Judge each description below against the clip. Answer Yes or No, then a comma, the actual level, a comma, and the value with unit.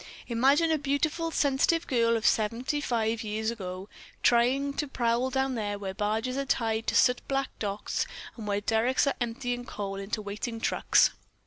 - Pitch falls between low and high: No, high, 235 Hz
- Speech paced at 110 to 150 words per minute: No, average, 165 wpm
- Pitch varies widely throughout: No, average, 3.8 semitones